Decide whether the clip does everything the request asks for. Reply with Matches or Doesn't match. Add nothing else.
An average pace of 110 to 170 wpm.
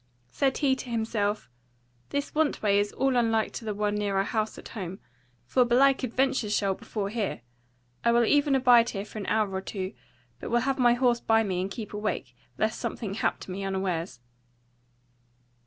Doesn't match